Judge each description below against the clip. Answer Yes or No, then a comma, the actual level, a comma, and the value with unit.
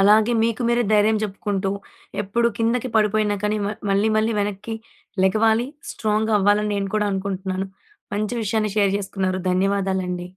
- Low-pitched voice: No, high, 210 Hz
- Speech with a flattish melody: Yes, narrow, 2.1 semitones